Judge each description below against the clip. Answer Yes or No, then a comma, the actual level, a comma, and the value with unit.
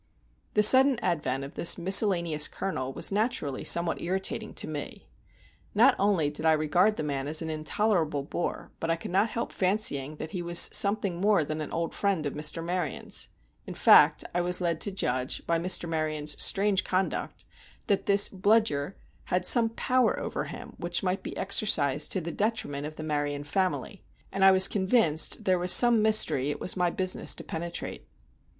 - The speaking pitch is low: No, medium, 175 Hz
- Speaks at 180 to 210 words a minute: Yes, average, 185 wpm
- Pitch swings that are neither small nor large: Yes, average, 4.5 semitones